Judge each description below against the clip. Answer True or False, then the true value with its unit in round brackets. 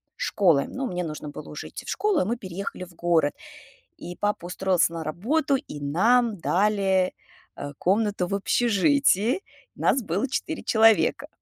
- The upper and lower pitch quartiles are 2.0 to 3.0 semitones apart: False (5.1 semitones)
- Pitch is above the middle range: True (195 Hz)